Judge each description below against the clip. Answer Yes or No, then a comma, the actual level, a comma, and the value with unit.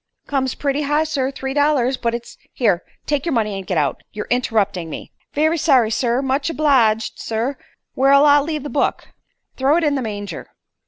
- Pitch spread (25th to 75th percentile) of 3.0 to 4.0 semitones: No, average, 4.5 semitones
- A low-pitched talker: No, very high, 265 Hz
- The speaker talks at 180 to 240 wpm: Yes, average, 195 wpm